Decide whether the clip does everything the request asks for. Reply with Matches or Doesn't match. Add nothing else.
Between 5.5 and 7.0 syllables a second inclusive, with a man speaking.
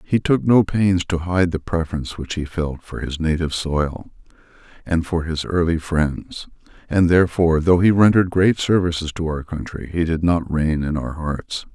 Doesn't match